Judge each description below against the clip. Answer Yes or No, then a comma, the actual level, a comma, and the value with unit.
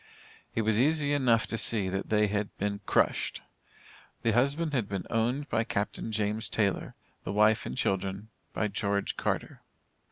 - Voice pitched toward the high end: No, low, 110 Hz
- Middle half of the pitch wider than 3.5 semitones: No, average, 2.7 semitones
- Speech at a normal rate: Yes, average, 160 wpm